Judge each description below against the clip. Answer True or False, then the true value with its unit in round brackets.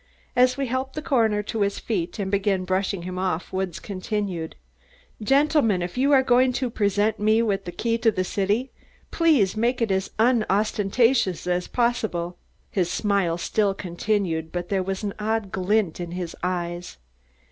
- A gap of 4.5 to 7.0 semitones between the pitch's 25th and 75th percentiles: False (3.9 semitones)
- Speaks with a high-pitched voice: True (200 Hz)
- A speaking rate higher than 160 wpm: True (170 wpm)